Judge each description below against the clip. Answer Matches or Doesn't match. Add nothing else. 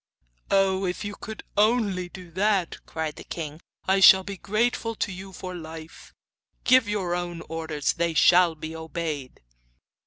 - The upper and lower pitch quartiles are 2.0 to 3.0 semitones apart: Doesn't match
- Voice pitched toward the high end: Doesn't match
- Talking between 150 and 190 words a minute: Matches